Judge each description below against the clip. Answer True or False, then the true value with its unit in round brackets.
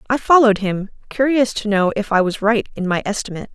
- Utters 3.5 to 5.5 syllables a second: False (6.3 syllables/s)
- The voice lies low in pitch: False (215 Hz)